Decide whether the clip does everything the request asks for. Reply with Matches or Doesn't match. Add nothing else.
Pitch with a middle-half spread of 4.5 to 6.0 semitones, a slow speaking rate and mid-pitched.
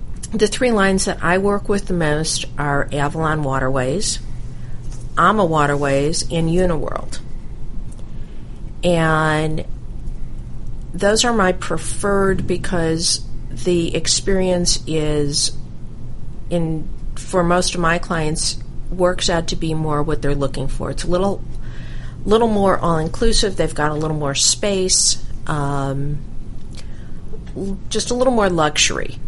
Matches